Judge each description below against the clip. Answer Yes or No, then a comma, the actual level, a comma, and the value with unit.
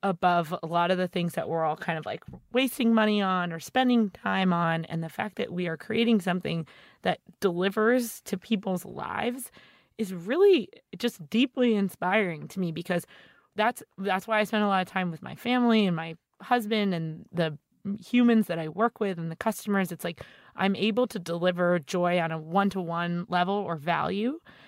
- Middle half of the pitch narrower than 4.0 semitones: No, average, 4.3 semitones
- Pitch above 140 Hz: Yes, high, 190 Hz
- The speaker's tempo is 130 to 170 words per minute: No, average, 195 wpm